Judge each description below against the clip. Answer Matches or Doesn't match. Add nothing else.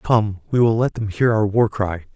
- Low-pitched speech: Matches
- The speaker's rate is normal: Doesn't match